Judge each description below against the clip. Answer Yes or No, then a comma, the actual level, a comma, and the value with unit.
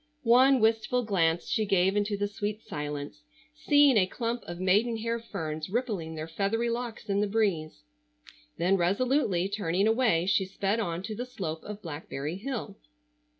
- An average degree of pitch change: Yes, average, 5.0 semitones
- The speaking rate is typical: Yes, average, 160 wpm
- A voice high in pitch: Yes, high, 205 Hz